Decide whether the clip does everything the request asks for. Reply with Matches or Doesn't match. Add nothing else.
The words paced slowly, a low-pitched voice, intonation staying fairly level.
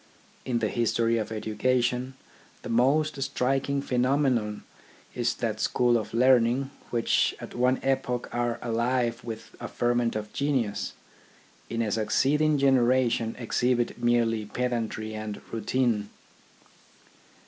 Matches